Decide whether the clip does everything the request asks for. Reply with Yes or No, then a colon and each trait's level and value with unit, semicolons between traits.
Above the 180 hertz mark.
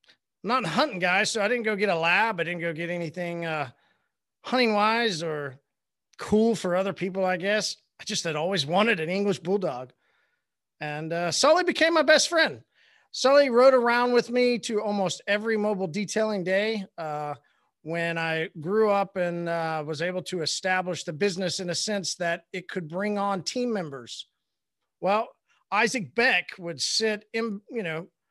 Yes: high, 190 Hz